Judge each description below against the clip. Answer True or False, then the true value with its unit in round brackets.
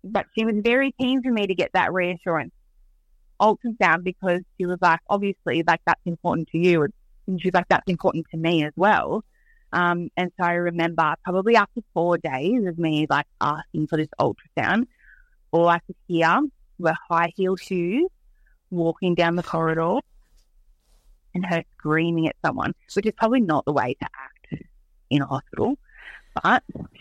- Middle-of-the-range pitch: True (175 Hz)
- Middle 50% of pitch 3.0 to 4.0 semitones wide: True (3.7 semitones)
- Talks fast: False (170 wpm)